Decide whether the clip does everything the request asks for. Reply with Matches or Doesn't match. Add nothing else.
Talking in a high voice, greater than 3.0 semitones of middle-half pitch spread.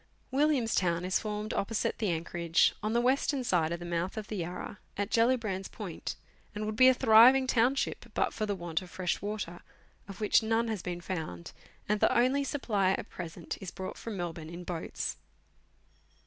Matches